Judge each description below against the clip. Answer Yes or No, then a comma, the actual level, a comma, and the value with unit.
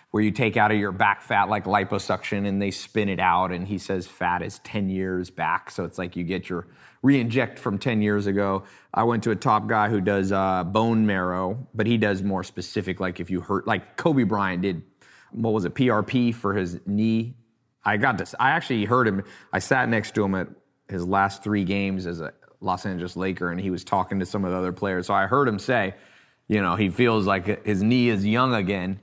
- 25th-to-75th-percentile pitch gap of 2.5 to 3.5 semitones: Yes, average, 2.8 semitones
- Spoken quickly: Yes, fast, 235 wpm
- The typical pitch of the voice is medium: No, low, 100 Hz